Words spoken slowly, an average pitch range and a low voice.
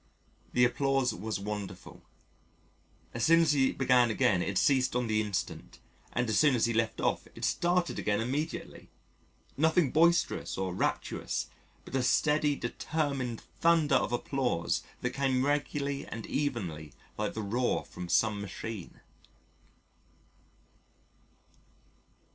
Yes: slow, 130 wpm; average, 4.9 semitones; low, 125 Hz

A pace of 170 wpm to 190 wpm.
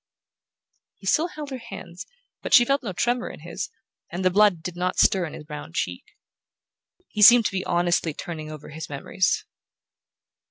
Yes: average, 175 wpm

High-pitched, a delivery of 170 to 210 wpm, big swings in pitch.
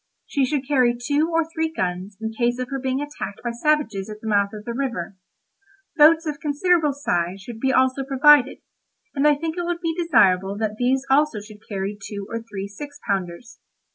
Yes: very high, 255 Hz; average, 200 wpm; wide, 6.0 semitones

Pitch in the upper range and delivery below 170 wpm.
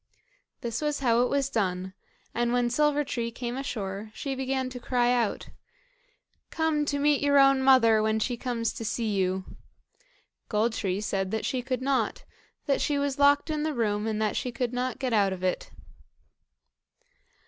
No: high, 245 Hz; average, 180 wpm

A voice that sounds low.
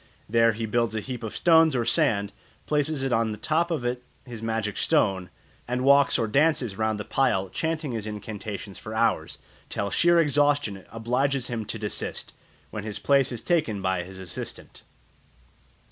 Yes: low, 115 Hz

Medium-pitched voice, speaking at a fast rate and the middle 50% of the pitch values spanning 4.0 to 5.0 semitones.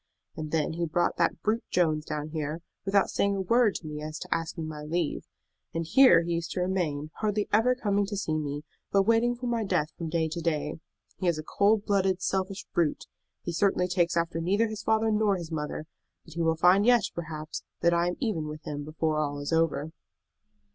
Yes: medium, 170 Hz; fast, 215 wpm; average, 4.4 semitones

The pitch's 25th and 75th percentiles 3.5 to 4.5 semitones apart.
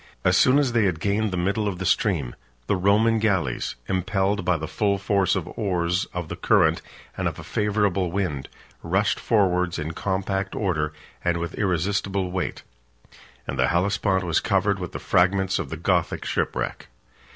No: narrow, 2.5 semitones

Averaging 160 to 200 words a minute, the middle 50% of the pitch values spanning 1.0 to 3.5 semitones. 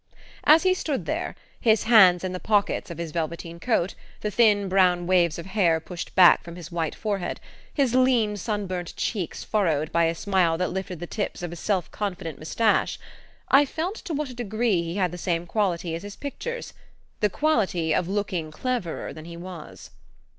No: average, 190 wpm; average, 4.3 semitones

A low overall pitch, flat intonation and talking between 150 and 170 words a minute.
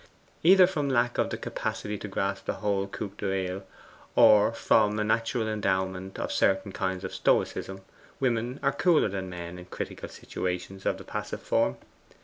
No: low, 100 Hz; average, 3.3 semitones; average, 165 wpm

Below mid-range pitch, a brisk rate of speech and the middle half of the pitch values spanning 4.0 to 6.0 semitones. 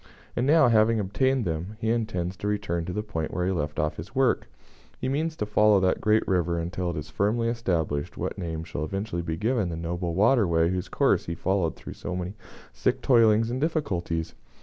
Yes: very low, 95 Hz; fast, 210 wpm; average, 4.9 semitones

